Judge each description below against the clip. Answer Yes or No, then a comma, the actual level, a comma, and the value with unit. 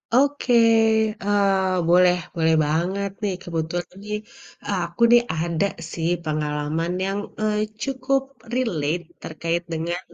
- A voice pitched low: No, medium, 175 Hz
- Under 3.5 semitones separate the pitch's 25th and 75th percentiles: No, average, 4.0 semitones